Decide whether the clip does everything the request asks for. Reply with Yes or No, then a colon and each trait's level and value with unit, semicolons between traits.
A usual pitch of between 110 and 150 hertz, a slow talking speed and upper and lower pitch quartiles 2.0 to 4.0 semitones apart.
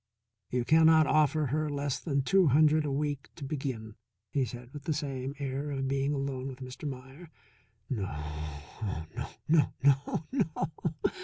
No: medium, 140 Hz; average, 160 wpm; average, 2.8 semitones